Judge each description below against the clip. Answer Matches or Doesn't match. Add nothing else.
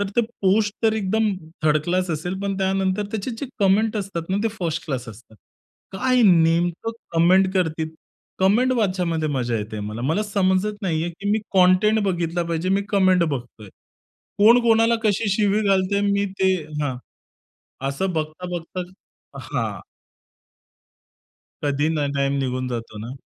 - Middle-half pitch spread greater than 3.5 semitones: Matches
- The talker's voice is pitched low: Doesn't match